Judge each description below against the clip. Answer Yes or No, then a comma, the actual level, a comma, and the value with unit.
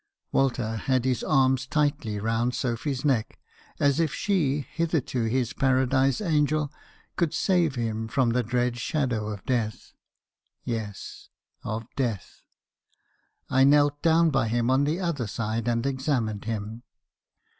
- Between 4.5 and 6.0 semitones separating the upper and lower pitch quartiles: No, average, 4.1 semitones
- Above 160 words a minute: No, slow, 135 wpm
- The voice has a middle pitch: No, low, 130 Hz